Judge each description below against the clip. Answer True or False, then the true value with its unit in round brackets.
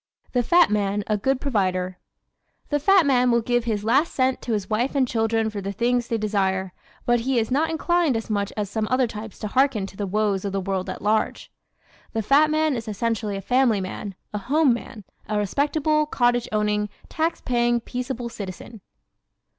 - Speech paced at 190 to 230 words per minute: True (200 wpm)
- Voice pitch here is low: False (230 Hz)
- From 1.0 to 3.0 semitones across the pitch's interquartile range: False (4.0 semitones)